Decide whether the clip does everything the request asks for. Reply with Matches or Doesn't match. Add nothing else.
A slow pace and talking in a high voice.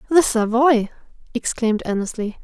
Matches